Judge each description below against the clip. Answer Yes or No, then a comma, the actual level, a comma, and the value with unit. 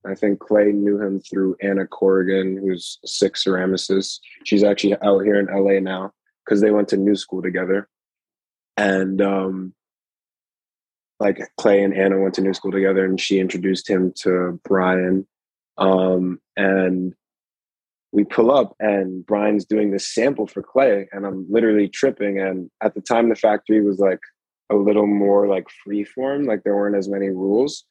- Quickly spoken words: No, average, 170 wpm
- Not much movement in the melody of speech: Yes, narrow, 1.4 semitones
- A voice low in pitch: Yes, low, 100 Hz